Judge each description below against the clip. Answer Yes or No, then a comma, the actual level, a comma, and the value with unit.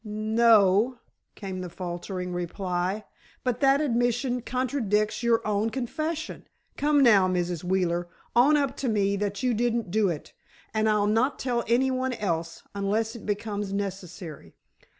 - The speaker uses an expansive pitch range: No, average, 4.3 semitones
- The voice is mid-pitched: No, high, 215 Hz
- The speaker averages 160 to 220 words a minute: No, average, 145 wpm